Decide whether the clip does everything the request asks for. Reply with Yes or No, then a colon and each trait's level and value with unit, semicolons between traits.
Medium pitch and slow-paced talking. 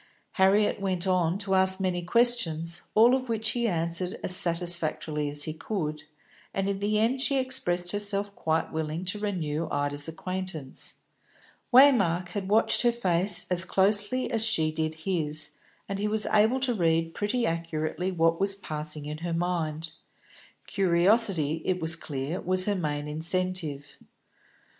No: medium, 180 Hz; average, 150 wpm